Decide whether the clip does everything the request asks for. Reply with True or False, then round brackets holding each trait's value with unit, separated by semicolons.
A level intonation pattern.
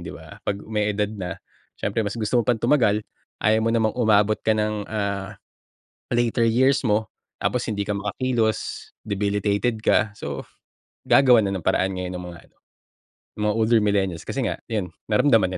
True (2.1 semitones)